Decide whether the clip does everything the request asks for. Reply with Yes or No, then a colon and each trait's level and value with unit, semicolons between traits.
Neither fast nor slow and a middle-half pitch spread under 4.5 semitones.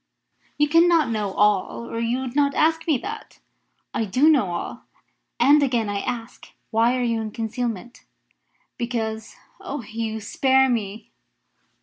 Yes: average, 145 wpm; average, 4.0 semitones